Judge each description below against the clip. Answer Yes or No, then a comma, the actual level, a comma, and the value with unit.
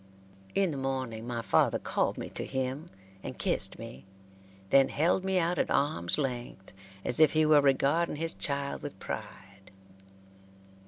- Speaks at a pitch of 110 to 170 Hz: Yes, medium, 140 Hz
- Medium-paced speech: Yes, average, 155 wpm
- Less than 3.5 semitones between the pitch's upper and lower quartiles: No, average, 4.3 semitones